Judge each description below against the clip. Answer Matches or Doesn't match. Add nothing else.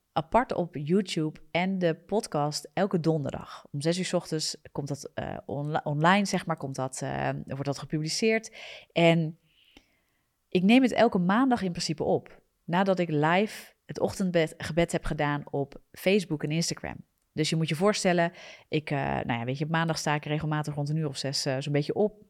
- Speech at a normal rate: Matches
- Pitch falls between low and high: Matches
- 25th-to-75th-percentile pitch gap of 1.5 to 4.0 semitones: Matches